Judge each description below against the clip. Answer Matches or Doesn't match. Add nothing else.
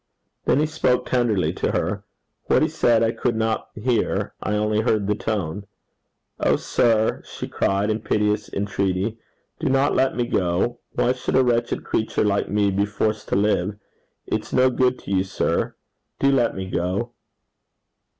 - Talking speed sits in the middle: Matches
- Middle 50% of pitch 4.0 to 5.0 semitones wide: Doesn't match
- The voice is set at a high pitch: Doesn't match